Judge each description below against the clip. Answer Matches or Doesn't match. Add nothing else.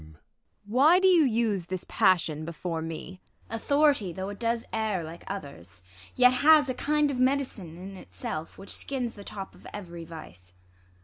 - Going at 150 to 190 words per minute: Matches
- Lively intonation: Matches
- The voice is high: Matches